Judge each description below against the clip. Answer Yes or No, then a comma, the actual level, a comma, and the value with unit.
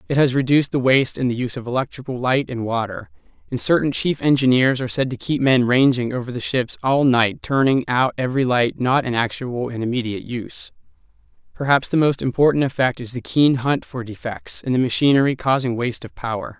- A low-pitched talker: Yes, low, 130 Hz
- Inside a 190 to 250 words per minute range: Yes, average, 200 wpm